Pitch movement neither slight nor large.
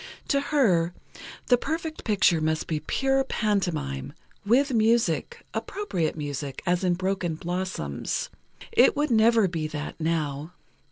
No: wide, 7.5 semitones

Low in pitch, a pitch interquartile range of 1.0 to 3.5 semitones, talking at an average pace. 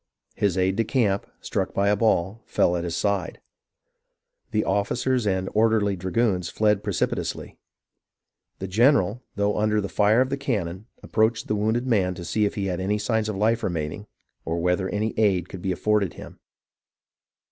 Yes: low, 105 Hz; average, 2.8 semitones; average, 170 wpm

